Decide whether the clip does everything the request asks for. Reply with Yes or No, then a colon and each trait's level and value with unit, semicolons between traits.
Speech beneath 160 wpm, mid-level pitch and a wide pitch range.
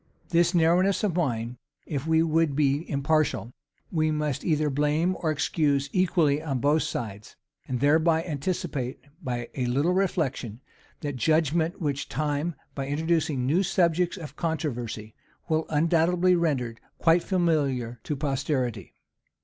No: slow, 135 wpm; medium, 155 Hz; average, 3.5 semitones